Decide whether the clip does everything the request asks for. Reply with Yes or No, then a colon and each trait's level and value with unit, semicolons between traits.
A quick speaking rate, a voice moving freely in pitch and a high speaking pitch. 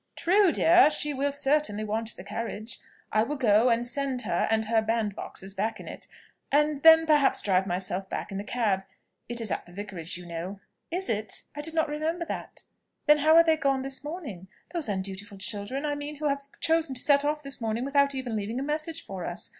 Yes: fast, 215 wpm; wide, 6.3 semitones; very high, 255 Hz